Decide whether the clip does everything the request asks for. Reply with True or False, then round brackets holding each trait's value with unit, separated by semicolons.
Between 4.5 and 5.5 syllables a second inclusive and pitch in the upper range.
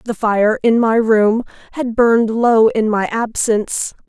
False (4.0 syllables/s; 225 Hz)